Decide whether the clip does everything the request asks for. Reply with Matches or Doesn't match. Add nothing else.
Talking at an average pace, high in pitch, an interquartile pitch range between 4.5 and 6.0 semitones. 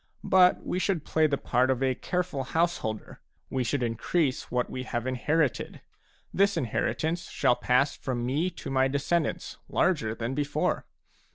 Doesn't match